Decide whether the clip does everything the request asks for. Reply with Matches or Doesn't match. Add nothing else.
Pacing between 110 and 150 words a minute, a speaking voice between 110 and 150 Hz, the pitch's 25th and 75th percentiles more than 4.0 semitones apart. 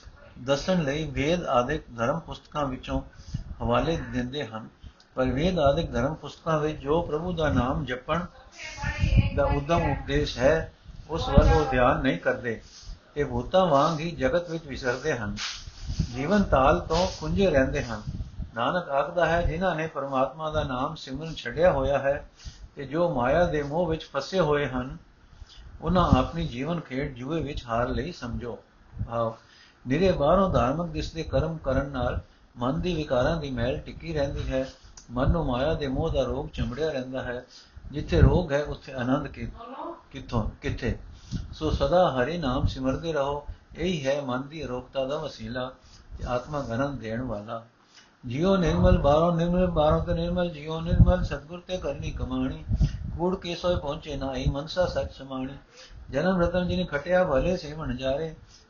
Doesn't match